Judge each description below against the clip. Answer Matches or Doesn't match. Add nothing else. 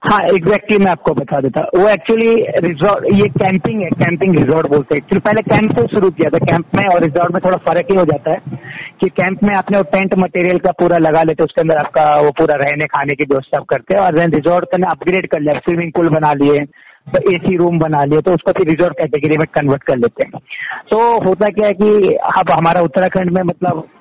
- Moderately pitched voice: Matches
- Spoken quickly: Matches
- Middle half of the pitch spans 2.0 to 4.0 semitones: Matches